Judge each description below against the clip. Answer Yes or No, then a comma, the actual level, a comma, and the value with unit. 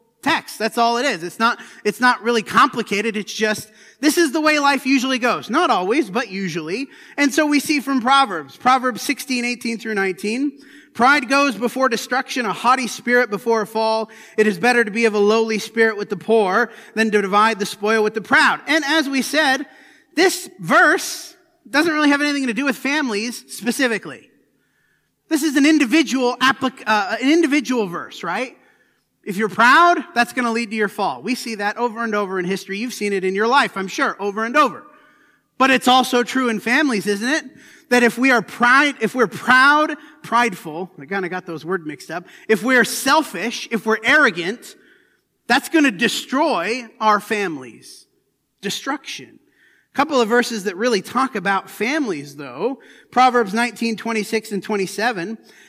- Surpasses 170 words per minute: Yes, average, 185 wpm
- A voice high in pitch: Yes, high, 240 Hz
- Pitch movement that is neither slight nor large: Yes, average, 4.7 semitones